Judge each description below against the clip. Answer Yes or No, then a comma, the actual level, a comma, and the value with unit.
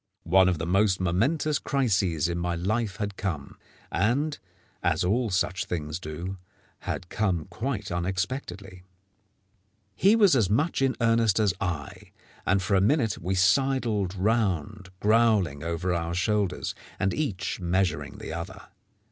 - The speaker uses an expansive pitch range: No, average, 4.1 semitones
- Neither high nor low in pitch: No, very low, 95 Hz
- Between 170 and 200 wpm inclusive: No, average, 140 wpm